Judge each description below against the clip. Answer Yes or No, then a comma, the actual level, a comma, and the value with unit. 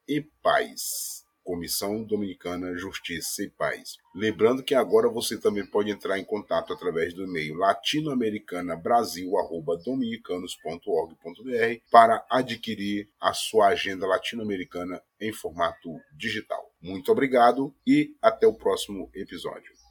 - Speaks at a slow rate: Yes, slow, 110 wpm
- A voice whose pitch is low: Yes, low, 115 Hz